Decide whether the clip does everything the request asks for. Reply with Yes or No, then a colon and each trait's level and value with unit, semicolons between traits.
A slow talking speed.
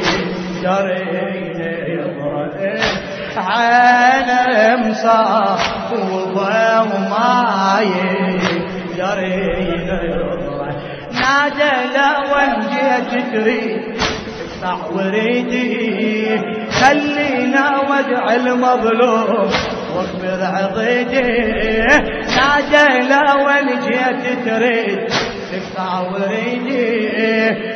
Yes: slow, 50 wpm